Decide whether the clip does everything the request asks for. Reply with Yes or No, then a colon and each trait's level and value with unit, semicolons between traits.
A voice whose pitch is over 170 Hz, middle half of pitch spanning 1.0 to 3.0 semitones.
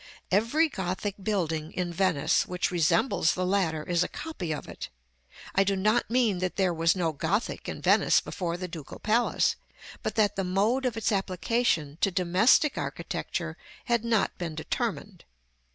No: high, 190 Hz; average, 4.1 semitones